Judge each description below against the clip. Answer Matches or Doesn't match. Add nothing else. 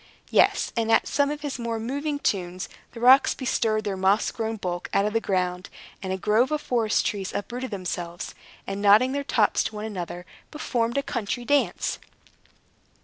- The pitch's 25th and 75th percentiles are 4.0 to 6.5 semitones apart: Matches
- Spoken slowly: Doesn't match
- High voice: Matches